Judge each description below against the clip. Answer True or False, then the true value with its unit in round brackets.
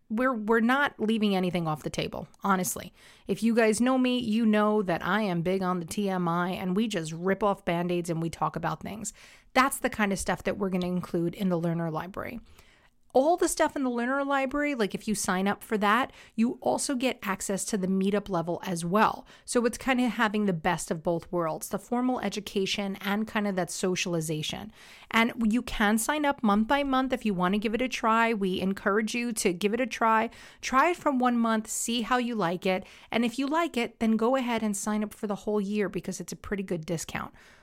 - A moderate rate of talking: False (230 wpm)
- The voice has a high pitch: True (210 Hz)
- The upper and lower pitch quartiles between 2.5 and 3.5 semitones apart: False (4.1 semitones)